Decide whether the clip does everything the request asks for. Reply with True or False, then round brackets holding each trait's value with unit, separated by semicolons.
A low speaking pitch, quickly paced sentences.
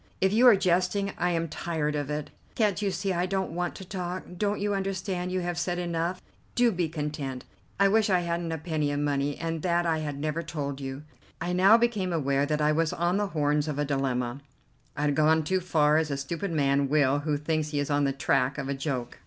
False (160 Hz; 235 wpm)